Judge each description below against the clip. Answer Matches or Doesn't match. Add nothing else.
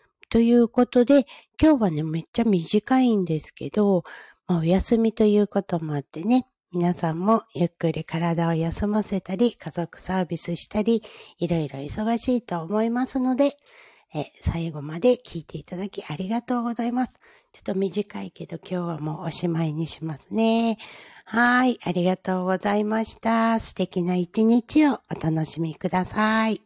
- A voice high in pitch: Matches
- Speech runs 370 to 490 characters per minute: Doesn't match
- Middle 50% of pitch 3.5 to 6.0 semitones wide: Matches